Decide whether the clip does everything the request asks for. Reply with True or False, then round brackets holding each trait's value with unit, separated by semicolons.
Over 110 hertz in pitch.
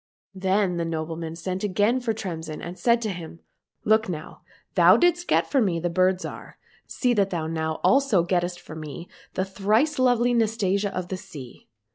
True (185 Hz)